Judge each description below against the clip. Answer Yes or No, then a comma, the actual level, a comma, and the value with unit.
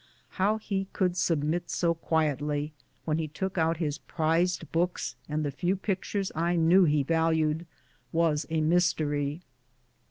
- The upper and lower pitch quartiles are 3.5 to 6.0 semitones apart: No, narrow, 2.5 semitones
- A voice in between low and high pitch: Yes, medium, 165 Hz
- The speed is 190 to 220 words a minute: No, average, 150 wpm